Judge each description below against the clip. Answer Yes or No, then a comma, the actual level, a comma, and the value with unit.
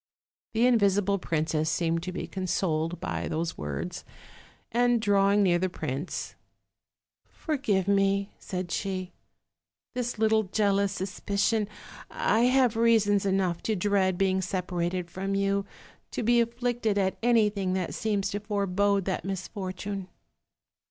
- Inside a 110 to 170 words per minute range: Yes, slow, 135 wpm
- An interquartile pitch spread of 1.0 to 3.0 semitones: Yes, narrow, 2.6 semitones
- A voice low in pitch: No, high, 195 Hz